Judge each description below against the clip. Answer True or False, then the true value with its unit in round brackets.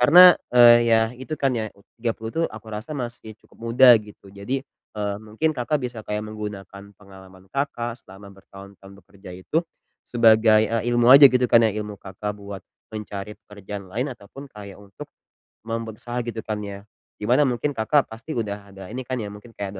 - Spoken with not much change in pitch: False (3.3 semitones)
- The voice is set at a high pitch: False (110 Hz)